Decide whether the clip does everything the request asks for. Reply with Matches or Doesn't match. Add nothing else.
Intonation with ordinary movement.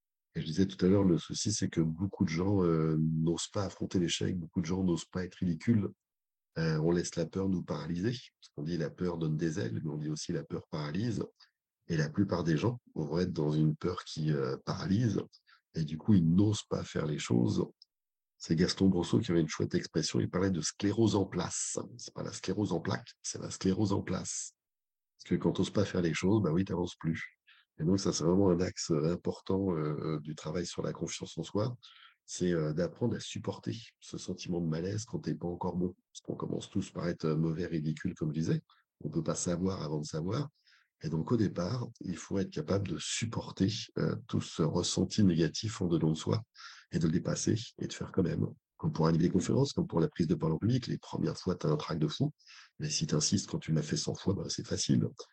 Matches